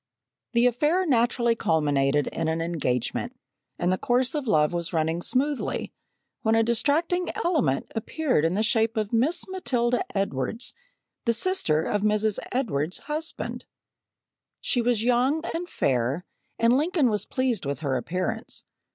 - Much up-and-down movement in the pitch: Yes, wide, 8.0 semitones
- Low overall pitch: No, high, 230 Hz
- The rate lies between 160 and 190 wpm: No, average, 145 wpm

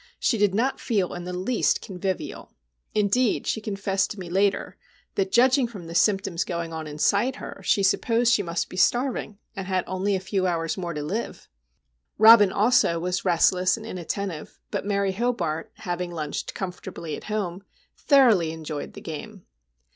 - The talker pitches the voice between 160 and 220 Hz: Yes, high, 190 Hz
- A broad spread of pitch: No, average, 3.7 semitones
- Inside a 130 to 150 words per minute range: No, average, 170 wpm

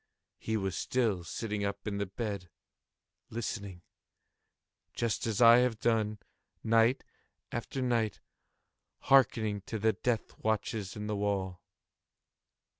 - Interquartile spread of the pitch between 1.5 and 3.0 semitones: Yes, narrow, 2.4 semitones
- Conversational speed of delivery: No, slow, 115 wpm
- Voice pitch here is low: Yes, low, 110 Hz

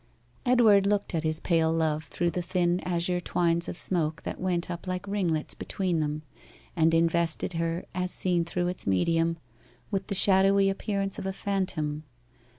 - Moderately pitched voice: Yes, medium, 175 Hz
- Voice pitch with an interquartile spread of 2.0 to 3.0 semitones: Yes, narrow, 2.6 semitones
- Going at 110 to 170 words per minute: Yes, average, 165 wpm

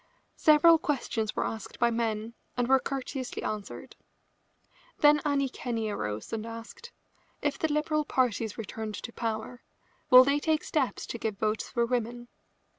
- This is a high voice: Yes, high, 240 Hz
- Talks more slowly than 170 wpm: Yes, average, 155 wpm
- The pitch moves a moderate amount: Yes, average, 4.3 semitones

